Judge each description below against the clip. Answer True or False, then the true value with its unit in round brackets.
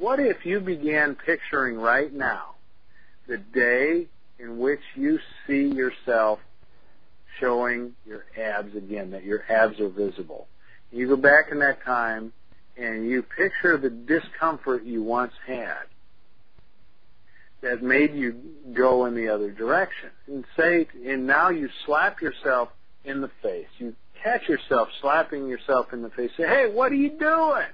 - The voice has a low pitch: True (125 Hz)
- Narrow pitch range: False (5.0 semitones)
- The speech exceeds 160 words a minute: False (150 wpm)